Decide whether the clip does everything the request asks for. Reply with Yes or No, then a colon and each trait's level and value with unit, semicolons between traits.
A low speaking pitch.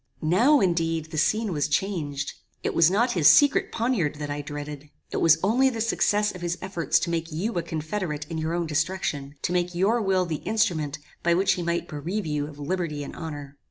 No: medium, 170 Hz